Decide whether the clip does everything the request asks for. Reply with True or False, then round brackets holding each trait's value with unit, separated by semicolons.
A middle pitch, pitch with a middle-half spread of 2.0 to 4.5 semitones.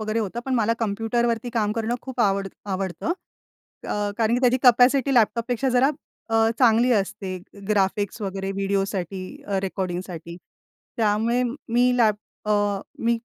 False (220 Hz; 3.4 semitones)